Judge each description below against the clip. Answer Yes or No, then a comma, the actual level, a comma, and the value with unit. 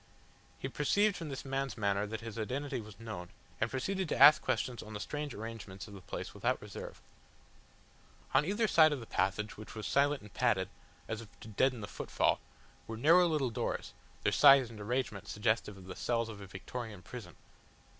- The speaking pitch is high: No, low, 115 Hz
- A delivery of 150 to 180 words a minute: No, average, 195 wpm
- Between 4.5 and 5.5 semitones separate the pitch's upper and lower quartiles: Yes, average, 4.8 semitones